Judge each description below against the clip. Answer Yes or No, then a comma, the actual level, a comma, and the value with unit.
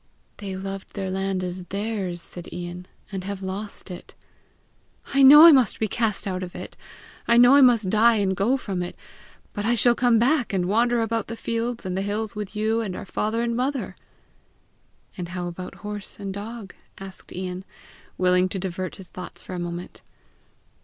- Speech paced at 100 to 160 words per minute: No, average, 190 wpm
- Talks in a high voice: Yes, high, 200 Hz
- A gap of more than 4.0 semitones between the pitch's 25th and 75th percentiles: No, average, 3.7 semitones